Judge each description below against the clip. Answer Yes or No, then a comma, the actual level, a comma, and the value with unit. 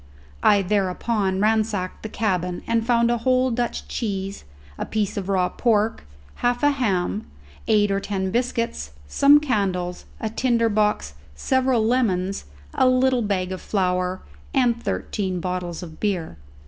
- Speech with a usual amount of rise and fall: Yes, average, 4.3 semitones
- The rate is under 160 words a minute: Yes, average, 145 wpm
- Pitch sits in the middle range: No, high, 210 Hz